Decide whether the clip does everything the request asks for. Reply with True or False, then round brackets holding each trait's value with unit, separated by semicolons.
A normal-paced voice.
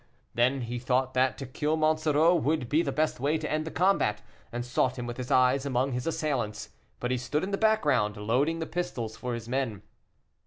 False (210 wpm)